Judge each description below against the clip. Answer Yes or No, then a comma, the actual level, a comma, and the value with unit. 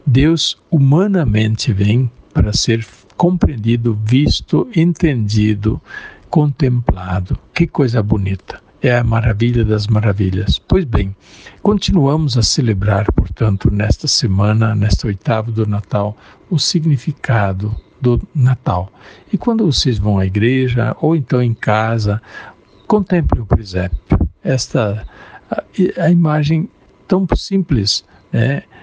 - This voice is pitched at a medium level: No, low, 115 Hz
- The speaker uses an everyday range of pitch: No, wide, 6.2 semitones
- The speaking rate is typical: No, slow, 110 wpm